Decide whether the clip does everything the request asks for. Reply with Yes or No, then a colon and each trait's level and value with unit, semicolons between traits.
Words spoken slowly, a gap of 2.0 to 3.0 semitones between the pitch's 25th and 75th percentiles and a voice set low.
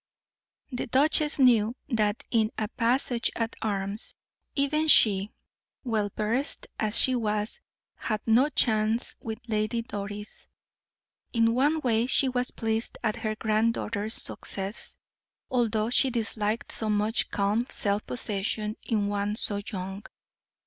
No: slow, 130 wpm; narrow, 2.4 semitones; high, 220 Hz